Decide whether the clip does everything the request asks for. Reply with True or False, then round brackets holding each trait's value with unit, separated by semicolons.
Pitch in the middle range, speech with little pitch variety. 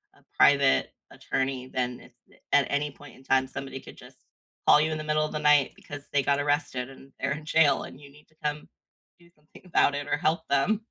True (145 Hz; 2.0 semitones)